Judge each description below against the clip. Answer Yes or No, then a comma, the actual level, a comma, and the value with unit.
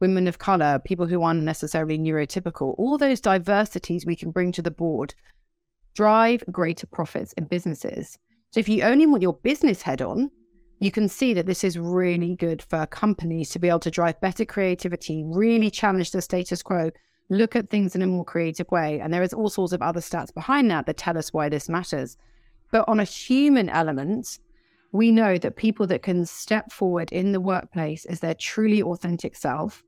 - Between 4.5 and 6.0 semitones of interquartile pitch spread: No, average, 4.0 semitones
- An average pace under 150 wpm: No, average, 195 wpm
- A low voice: No, medium, 180 Hz